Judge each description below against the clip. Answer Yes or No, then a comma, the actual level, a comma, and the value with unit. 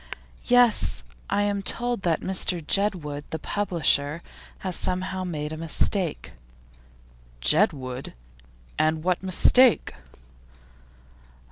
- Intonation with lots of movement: No, average, 4.5 semitones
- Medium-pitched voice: Yes, medium, 180 Hz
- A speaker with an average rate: No, slow, 95 wpm